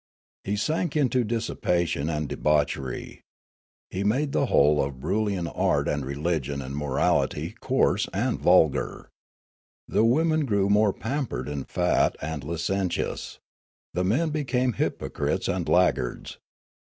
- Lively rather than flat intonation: Yes, wide, 8.4 semitones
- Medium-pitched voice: No, very low, 95 Hz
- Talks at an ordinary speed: No, slow, 125 wpm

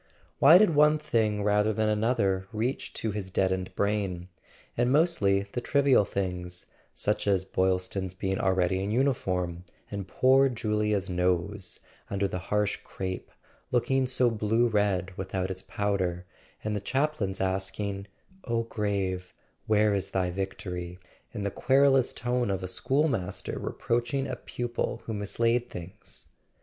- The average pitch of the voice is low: Yes, low, 100 Hz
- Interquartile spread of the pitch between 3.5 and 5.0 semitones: Yes, average, 4.1 semitones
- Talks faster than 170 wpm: No, average, 145 wpm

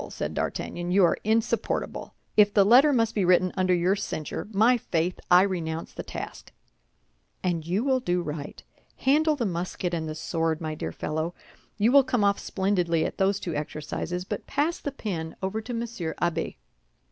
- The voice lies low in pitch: No, medium, 185 Hz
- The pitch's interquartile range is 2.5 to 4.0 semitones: No, average, 4.9 semitones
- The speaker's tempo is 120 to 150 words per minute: No, average, 180 wpm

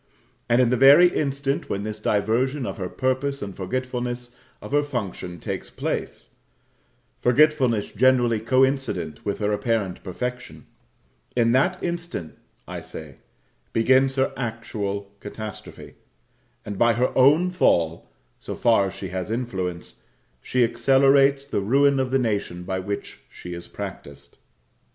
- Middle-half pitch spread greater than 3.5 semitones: Yes, average, 5.0 semitones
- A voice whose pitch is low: Yes, low, 120 Hz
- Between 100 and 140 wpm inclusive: Yes, slow, 135 wpm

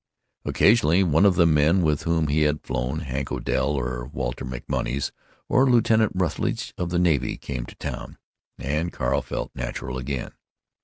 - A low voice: Yes, very low, 75 Hz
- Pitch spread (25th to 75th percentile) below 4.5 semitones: No, average, 5.1 semitones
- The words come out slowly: No, average, 150 wpm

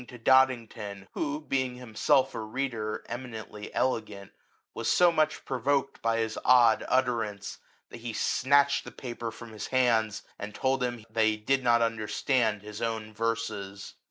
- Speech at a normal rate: Yes, average, 160 wpm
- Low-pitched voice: Yes, low, 115 Hz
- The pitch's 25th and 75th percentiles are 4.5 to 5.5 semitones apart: No, average, 3.2 semitones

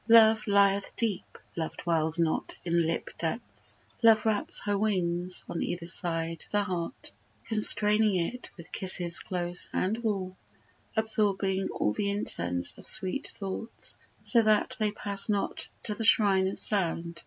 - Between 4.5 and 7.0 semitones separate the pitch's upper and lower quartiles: No, average, 3.7 semitones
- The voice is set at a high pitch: Yes, high, 195 Hz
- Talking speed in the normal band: Yes, average, 145 wpm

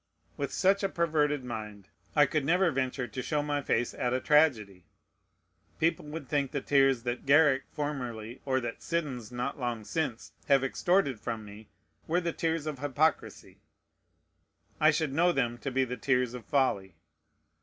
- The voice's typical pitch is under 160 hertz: Yes, low, 135 Hz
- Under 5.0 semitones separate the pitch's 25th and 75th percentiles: Yes, average, 3.9 semitones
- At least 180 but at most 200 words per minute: No, average, 165 wpm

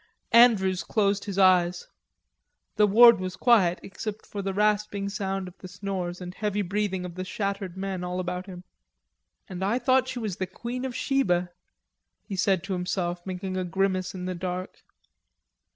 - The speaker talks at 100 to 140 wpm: No, average, 170 wpm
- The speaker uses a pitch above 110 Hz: Yes, high, 190 Hz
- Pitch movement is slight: Yes, narrow, 2.3 semitones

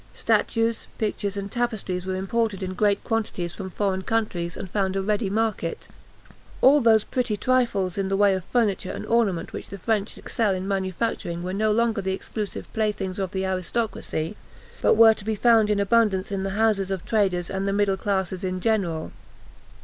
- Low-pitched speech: No, high, 200 Hz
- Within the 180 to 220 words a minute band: Yes, average, 185 wpm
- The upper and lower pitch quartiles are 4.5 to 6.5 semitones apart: No, average, 2.8 semitones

